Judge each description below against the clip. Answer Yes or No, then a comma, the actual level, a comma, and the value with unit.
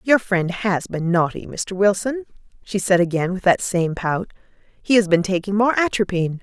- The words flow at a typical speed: Yes, average, 185 wpm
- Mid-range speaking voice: No, high, 195 Hz